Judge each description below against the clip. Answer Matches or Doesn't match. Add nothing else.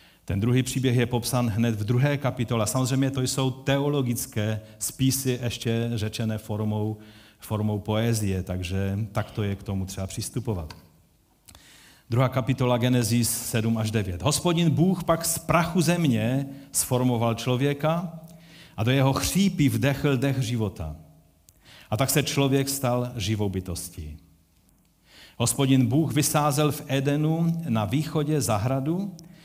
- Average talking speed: Matches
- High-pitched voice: Doesn't match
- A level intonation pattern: Doesn't match